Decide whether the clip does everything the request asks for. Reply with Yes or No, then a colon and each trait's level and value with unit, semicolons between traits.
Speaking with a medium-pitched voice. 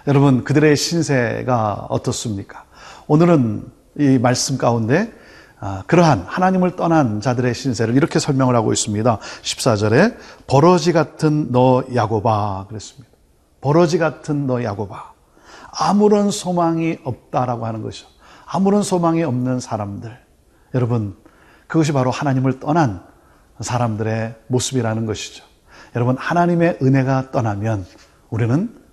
No: low, 125 Hz